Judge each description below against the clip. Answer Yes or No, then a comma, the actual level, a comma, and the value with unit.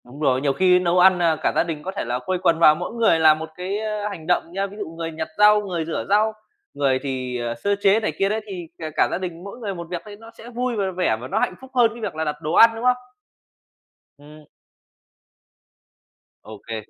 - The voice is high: No, medium, 180 Hz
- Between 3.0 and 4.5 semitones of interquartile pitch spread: No, average, 5.2 semitones